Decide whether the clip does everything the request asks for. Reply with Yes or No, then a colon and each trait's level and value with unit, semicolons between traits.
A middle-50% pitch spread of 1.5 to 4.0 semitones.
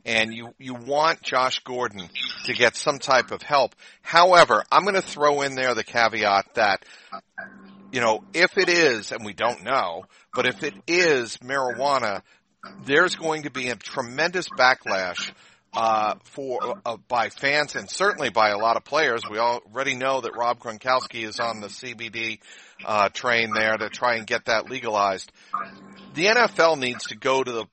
Yes: average, 3.1 semitones